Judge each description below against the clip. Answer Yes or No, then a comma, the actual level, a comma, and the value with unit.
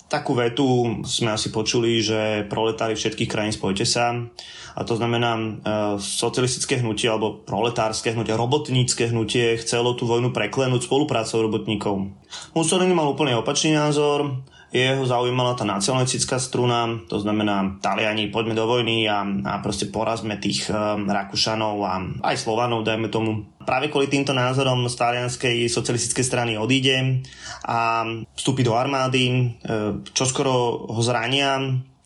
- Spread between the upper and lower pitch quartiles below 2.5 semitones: No, average, 2.8 semitones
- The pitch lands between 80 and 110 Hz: No, low, 120 Hz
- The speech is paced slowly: No, average, 135 wpm